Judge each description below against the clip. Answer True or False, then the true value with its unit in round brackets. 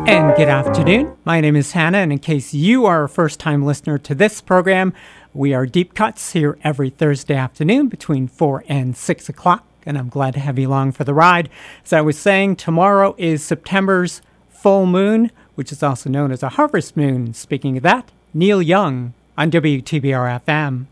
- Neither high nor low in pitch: True (155 Hz)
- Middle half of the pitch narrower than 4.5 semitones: False (4.9 semitones)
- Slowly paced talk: False (185 wpm)